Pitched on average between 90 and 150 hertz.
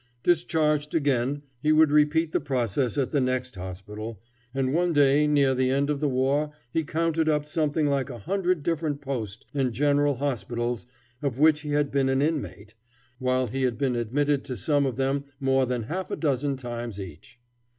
Yes: medium, 140 Hz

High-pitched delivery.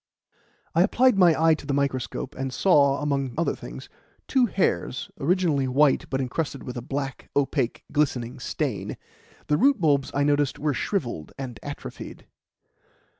No: medium, 140 Hz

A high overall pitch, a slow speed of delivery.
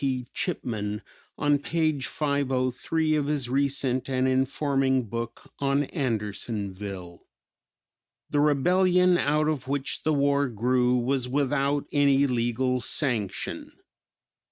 No: low, 135 Hz; slow, 105 wpm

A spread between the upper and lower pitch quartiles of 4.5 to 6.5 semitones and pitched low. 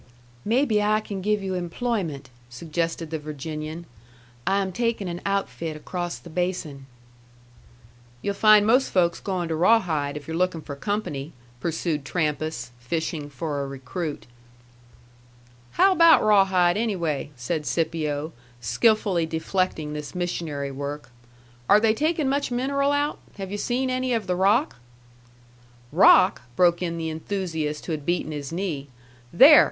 No: average, 5.3 semitones; medium, 175 Hz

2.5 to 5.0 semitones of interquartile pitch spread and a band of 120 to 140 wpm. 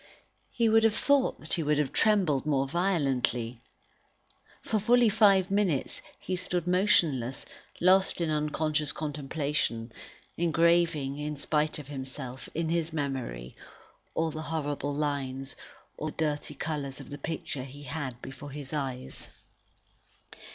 Yes: average, 3.9 semitones; slow, 135 wpm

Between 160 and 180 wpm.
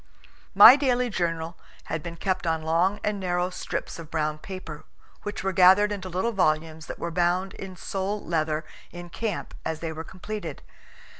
Yes: average, 170 wpm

